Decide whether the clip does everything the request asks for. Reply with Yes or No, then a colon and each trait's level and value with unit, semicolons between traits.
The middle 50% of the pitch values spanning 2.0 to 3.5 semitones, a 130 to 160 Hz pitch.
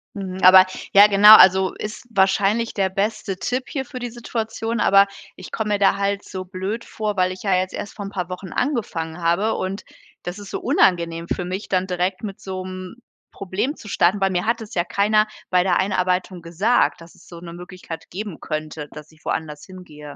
No: narrow, 2.6 semitones; high, 190 Hz